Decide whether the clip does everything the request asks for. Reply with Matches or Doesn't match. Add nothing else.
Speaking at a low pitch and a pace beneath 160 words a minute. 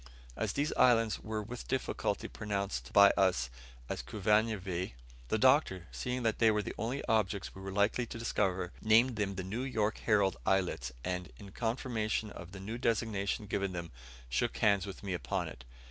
Doesn't match